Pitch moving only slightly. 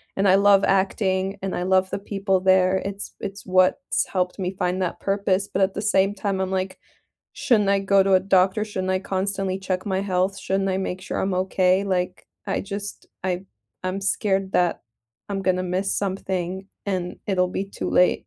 Yes: narrow, 1.1 semitones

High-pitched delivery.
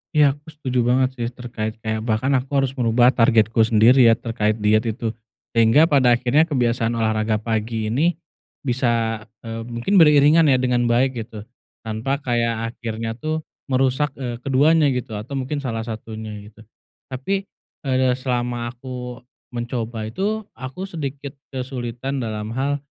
No: low, 120 Hz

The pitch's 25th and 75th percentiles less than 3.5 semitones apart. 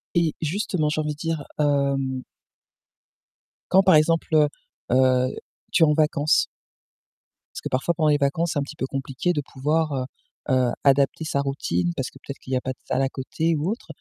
Yes: average, 3.1 semitones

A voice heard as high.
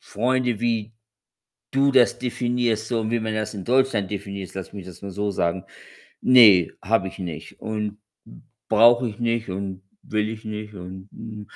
No: low, 110 Hz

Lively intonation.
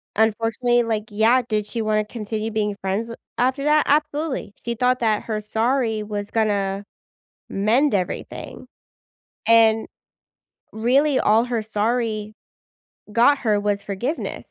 No: narrow, 2.6 semitones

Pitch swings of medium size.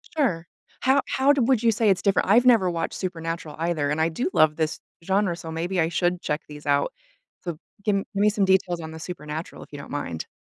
Yes: average, 4.2 semitones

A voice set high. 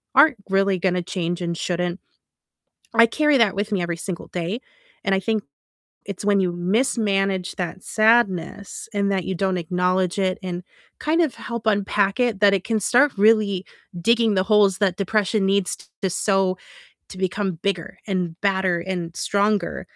Yes: high, 195 Hz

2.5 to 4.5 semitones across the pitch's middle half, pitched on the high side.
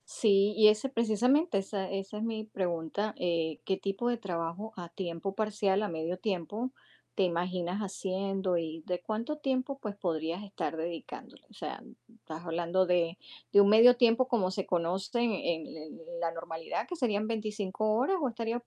Yes: average, 4.2 semitones; high, 200 Hz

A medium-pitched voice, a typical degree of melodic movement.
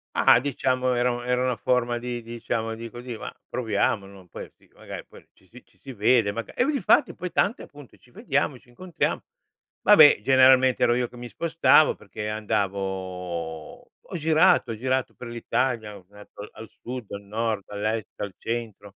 No: low, 120 Hz; average, 3.6 semitones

